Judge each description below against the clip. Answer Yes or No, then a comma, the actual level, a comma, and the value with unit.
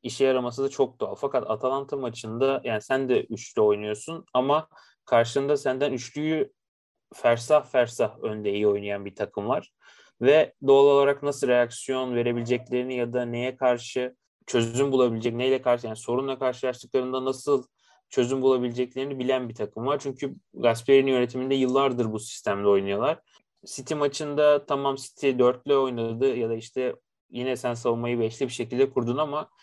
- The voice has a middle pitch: No, low, 130 Hz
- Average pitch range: No, narrow, 2.3 semitones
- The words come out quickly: Yes, fast, 150 wpm